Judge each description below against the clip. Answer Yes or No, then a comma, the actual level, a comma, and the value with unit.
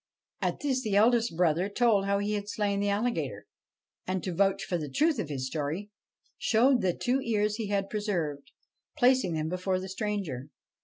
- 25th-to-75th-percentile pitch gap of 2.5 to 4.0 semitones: Yes, average, 3.6 semitones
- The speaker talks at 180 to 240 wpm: Yes, average, 190 wpm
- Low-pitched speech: No, high, 200 Hz